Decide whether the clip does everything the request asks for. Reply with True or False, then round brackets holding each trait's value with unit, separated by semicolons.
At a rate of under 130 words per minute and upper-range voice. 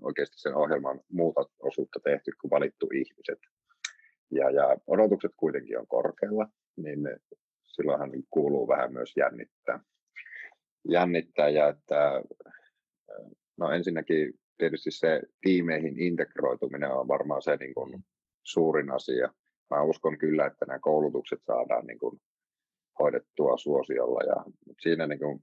True (120 wpm; 390 Hz)